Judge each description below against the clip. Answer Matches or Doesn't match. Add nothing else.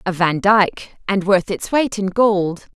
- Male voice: Doesn't match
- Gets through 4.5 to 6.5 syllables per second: Doesn't match